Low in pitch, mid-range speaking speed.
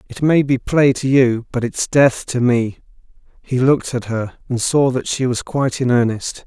No: low, 125 Hz; fast, 215 wpm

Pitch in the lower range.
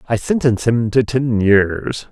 Yes: low, 115 Hz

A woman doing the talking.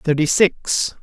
No: male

